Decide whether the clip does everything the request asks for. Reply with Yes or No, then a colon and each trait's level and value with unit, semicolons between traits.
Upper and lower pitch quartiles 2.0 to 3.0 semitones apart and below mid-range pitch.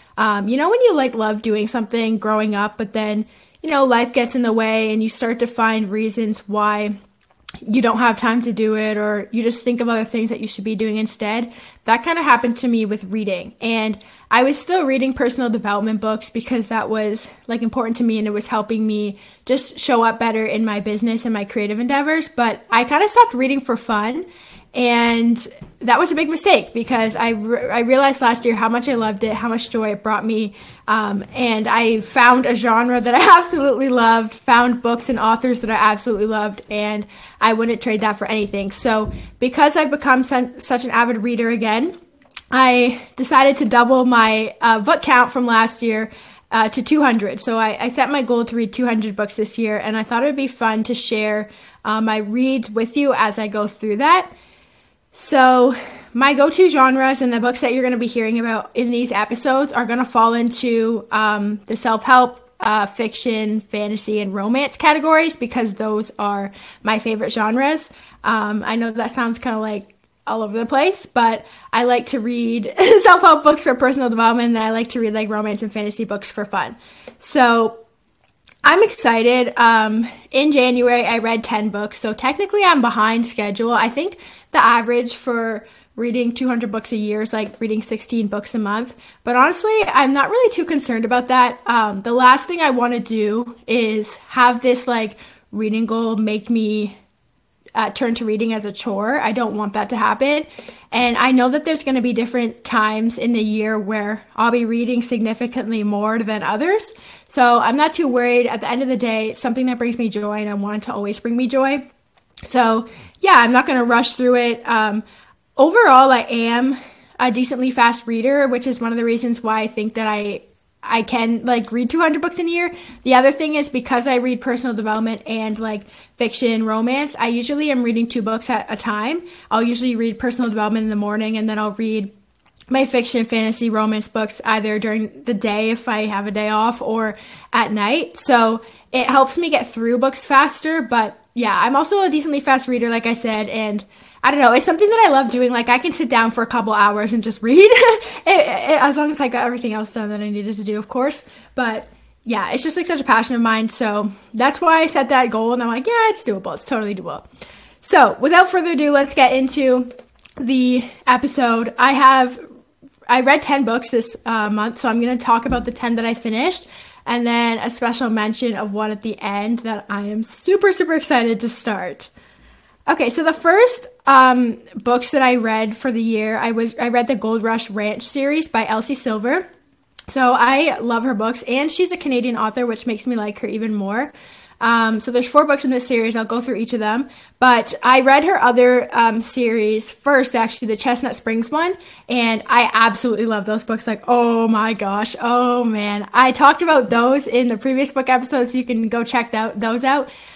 No: average, 2.7 semitones; high, 235 Hz